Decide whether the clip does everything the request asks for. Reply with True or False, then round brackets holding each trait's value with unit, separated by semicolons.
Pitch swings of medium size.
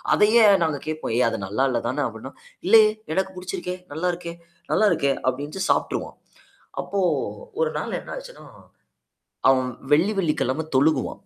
False (6.3 semitones)